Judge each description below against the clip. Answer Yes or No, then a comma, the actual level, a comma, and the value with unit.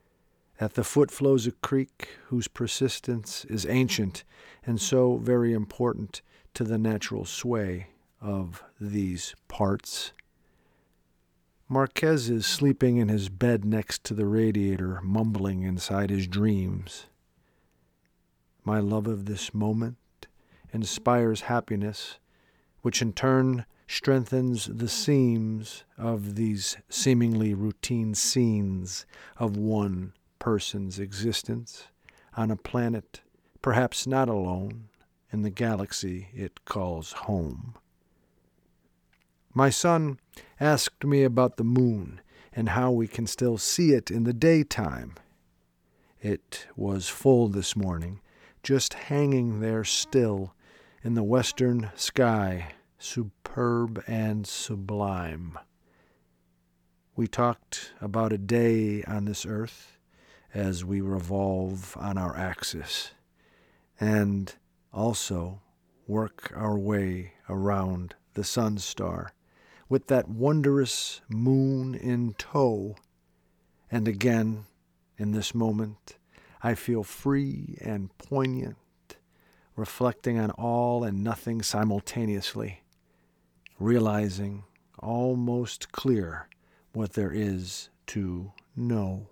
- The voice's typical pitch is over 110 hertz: No, low, 105 Hz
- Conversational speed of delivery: No, slow, 105 wpm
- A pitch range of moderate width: Yes, average, 4.2 semitones